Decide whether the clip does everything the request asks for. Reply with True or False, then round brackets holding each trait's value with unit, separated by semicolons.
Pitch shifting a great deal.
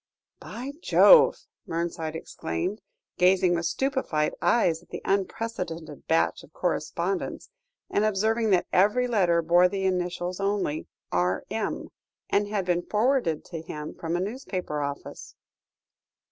False (4.1 semitones)